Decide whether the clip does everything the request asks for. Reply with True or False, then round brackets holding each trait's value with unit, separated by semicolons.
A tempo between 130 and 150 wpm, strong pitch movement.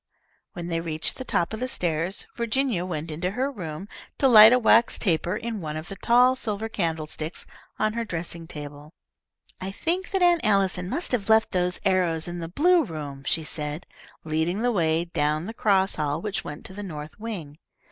False (195 wpm; 5.7 semitones)